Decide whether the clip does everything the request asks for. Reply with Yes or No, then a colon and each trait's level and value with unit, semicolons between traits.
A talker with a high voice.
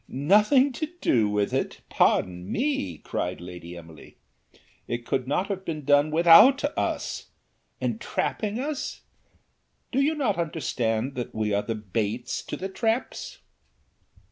No: medium, 145 Hz